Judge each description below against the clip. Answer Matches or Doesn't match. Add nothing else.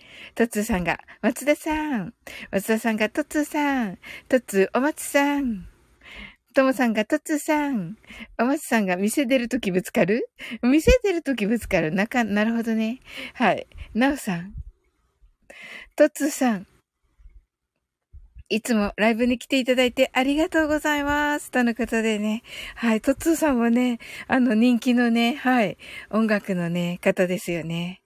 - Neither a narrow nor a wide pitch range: Matches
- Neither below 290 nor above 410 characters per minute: Matches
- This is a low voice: Doesn't match